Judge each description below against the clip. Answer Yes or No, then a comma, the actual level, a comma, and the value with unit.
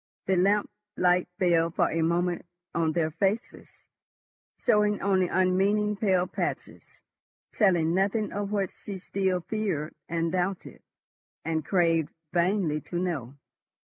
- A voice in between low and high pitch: Yes, medium, 180 Hz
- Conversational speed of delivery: No, slow, 125 wpm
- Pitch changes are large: No, average, 3.0 semitones